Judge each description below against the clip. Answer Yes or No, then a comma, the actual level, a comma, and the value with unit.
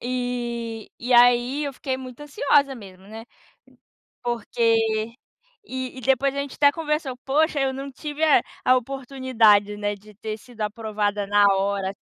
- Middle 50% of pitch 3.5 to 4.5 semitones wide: Yes, average, 4.1 semitones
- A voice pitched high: Yes, high, 245 Hz